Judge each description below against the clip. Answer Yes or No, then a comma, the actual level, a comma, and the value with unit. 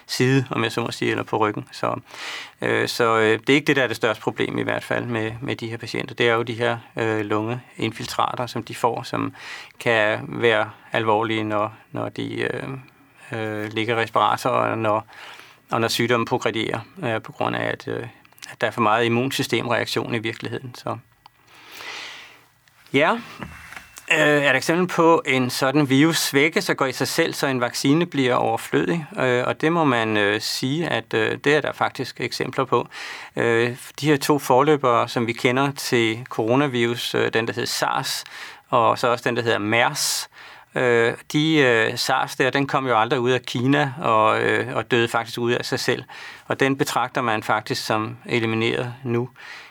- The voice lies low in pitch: Yes, low, 125 Hz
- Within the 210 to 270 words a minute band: No, average, 175 wpm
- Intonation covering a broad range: No, average, 3.5 semitones